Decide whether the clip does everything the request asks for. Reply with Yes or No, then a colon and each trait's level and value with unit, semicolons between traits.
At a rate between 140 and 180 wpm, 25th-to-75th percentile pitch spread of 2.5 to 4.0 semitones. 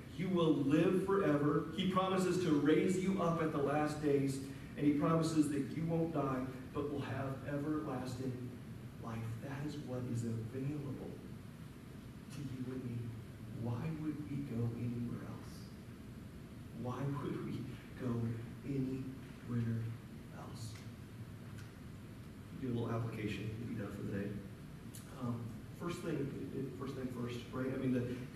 Yes: average, 145 wpm; average, 3.7 semitones